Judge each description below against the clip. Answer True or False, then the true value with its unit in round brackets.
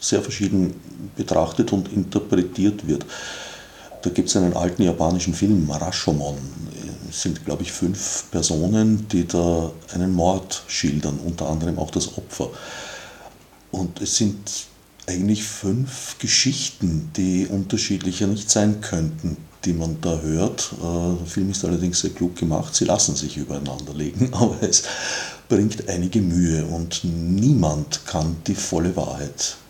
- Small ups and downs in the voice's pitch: False (3.4 semitones)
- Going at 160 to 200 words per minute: False (135 wpm)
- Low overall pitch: True (90 Hz)